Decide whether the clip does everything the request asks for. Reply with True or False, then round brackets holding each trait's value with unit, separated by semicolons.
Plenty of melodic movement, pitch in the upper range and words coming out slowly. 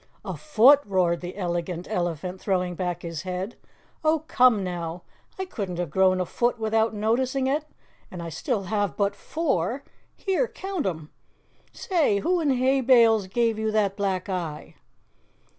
False (6.0 semitones; 205 Hz; 160 wpm)